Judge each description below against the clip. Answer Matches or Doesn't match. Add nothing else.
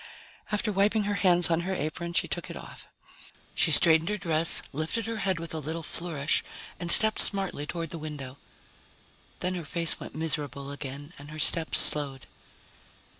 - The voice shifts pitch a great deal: Doesn't match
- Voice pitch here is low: Doesn't match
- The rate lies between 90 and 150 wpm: Doesn't match